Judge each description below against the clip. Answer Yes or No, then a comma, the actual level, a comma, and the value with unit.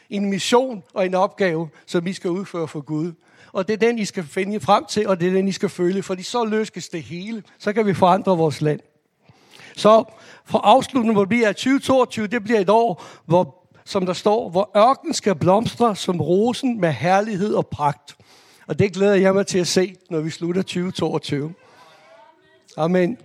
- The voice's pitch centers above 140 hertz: Yes, high, 190 Hz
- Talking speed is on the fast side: No, average, 195 wpm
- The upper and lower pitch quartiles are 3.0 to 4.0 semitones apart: Yes, average, 3.4 semitones